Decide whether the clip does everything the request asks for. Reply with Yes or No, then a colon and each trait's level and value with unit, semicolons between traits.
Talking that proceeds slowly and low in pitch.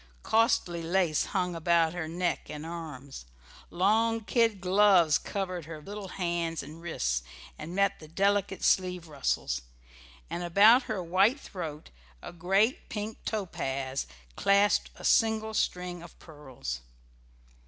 No: slow, 130 wpm; medium, 175 Hz